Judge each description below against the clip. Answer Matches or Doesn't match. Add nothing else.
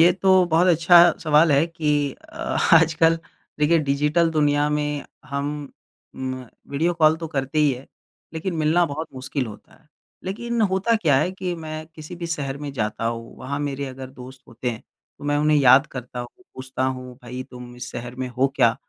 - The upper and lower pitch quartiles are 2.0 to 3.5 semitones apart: Doesn't match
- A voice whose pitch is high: Doesn't match